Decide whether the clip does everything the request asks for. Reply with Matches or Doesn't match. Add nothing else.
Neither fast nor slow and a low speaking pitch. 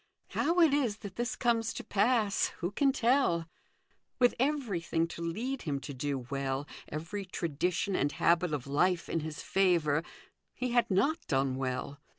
Doesn't match